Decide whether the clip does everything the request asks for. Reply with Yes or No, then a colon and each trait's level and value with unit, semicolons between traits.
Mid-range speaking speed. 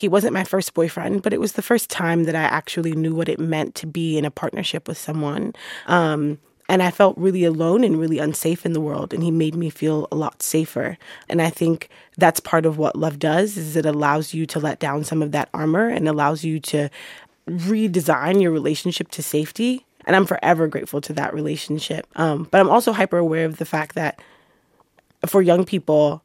No: fast, 215 wpm